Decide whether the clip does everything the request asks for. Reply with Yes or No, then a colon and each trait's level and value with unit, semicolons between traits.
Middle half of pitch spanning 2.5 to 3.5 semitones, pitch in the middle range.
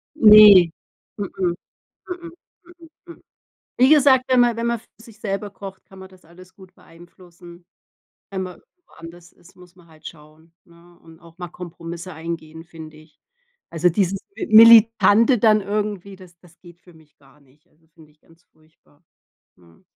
No: average, 4.0 semitones; medium, 175 Hz